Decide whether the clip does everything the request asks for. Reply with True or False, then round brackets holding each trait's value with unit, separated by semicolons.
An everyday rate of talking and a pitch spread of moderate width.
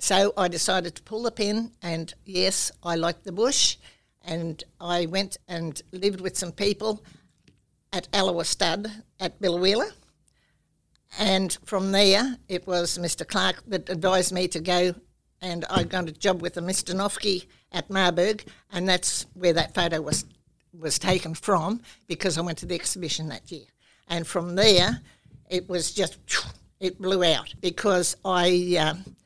False (160 wpm; 2.1 semitones)